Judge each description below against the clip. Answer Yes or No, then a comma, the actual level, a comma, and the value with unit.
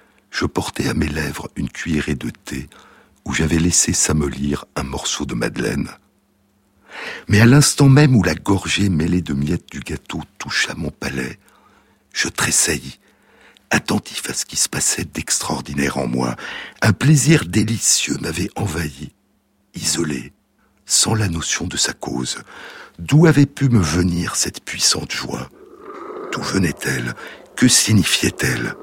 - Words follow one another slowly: Yes, slow, 140 wpm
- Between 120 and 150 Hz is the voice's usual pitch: No, very low, 90 Hz